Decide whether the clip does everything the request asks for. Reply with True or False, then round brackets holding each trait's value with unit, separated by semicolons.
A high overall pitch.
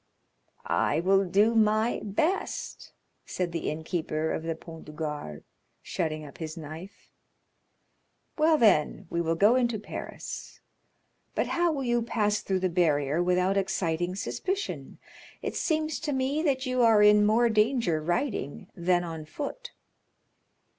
True (195 Hz)